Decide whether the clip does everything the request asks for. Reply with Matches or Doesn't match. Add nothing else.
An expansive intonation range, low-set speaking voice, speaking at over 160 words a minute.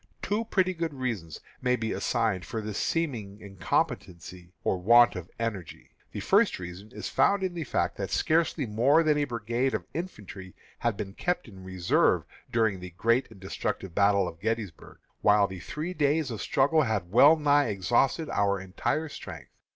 Matches